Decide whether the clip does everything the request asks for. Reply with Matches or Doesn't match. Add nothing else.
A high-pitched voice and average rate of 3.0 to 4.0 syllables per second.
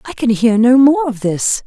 Doesn't match